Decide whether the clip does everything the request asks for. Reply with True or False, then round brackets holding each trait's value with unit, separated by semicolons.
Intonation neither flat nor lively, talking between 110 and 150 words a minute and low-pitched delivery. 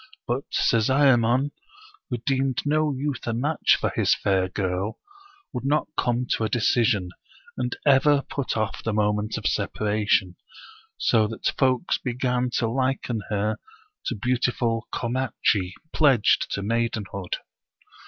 True (3.7 semitones; 135 wpm; 120 Hz)